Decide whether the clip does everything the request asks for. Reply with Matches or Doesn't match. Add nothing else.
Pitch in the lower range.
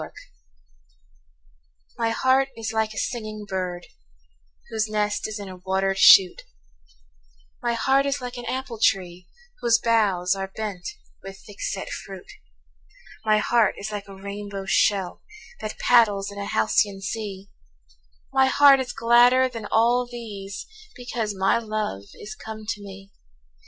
Doesn't match